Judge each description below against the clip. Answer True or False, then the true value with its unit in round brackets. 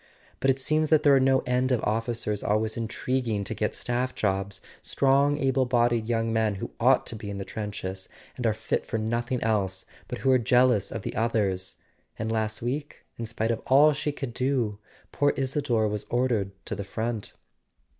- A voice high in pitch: False (115 Hz)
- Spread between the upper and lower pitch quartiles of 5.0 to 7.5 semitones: False (3.3 semitones)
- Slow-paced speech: False (190 wpm)